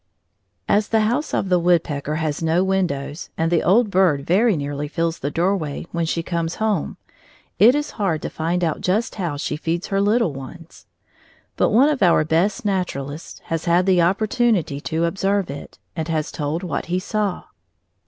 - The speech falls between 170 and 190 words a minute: Yes, average, 185 wpm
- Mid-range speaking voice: Yes, medium, 175 Hz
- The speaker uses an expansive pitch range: No, average, 3.8 semitones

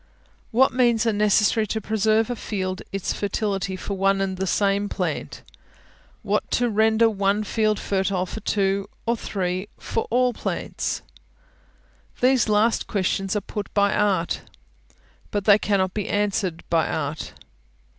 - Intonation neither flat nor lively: No, narrow, 2.2 semitones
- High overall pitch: Yes, high, 205 Hz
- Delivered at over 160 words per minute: No, average, 145 wpm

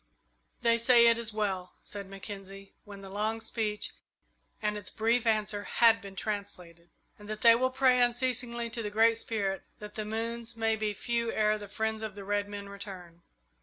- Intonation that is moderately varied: No, narrow, 2.3 semitones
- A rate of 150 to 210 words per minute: Yes, average, 185 wpm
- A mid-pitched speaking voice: No, high, 215 Hz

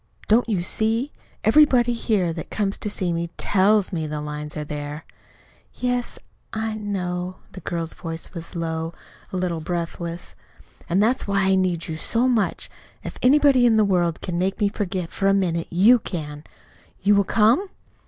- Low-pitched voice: No, high, 190 Hz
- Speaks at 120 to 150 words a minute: No, average, 175 wpm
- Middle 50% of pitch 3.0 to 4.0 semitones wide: No, average, 4.5 semitones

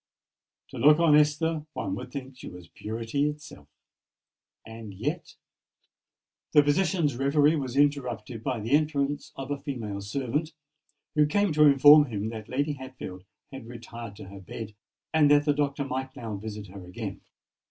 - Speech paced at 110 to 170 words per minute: Yes, average, 160 wpm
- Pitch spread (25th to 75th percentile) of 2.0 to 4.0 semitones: No, average, 4.8 semitones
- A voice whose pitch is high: No, low, 135 Hz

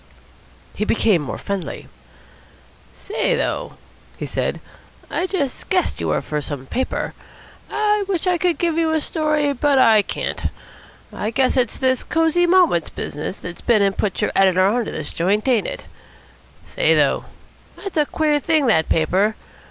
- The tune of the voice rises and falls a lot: Yes, wide, 8.6 semitones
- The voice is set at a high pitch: Yes, very high, 260 Hz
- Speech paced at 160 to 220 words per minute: Yes, average, 165 wpm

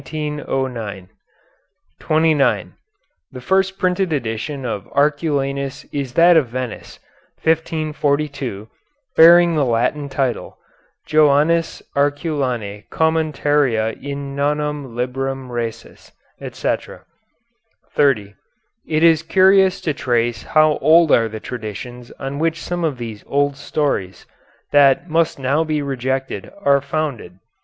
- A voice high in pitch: No, medium, 140 Hz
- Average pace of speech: No, slow, 115 wpm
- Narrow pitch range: No, average, 3.9 semitones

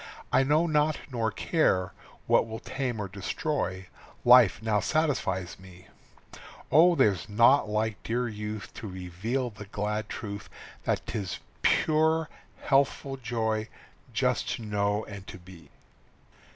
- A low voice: Yes, low, 110 Hz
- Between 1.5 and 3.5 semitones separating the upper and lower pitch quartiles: No, average, 4.8 semitones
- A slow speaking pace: Yes, slow, 130 wpm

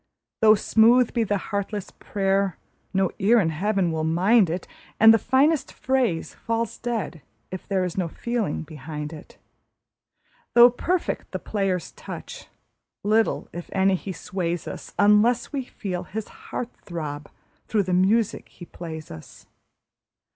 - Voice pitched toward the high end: Yes, high, 195 Hz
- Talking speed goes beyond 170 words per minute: No, average, 145 wpm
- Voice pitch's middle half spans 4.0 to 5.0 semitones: Yes, average, 4.6 semitones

